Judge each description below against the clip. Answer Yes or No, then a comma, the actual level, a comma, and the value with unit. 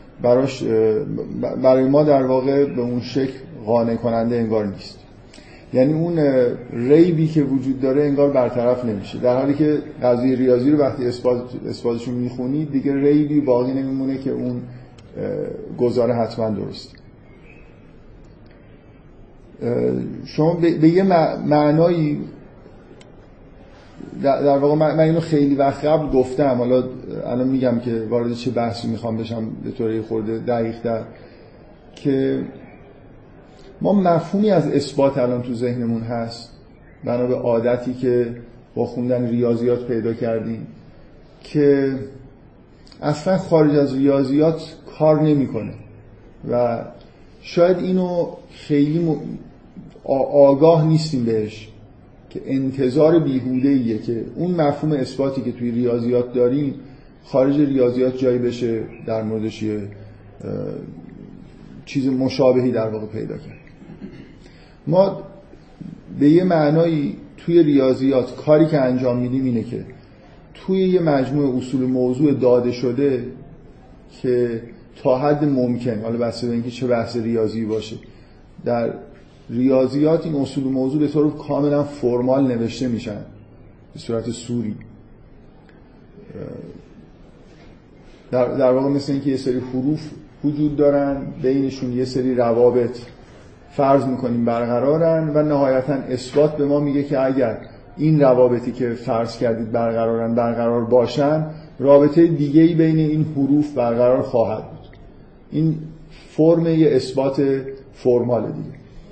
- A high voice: No, low, 130 Hz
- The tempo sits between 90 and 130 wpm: Yes, average, 120 wpm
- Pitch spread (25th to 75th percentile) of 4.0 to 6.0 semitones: No, average, 3.4 semitones